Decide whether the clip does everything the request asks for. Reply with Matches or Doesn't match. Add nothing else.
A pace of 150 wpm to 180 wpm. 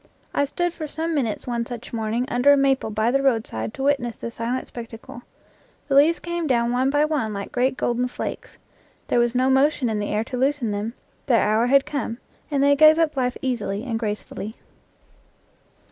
Doesn't match